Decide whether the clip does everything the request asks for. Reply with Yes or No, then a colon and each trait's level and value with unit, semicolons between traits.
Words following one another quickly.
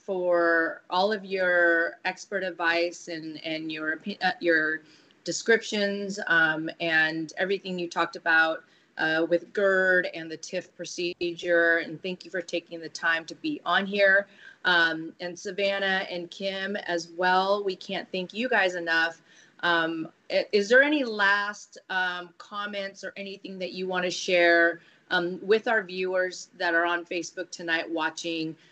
No: average, 155 wpm